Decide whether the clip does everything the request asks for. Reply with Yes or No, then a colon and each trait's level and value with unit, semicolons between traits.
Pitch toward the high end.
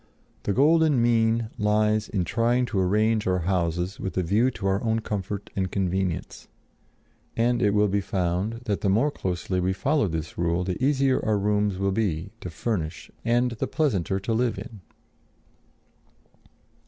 No: low, 105 Hz